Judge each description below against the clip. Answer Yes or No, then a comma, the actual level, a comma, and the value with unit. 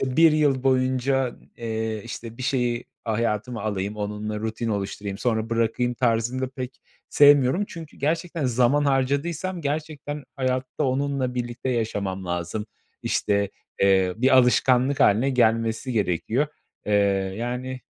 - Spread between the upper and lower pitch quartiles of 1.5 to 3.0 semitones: No, average, 3.4 semitones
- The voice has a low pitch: Yes, low, 125 Hz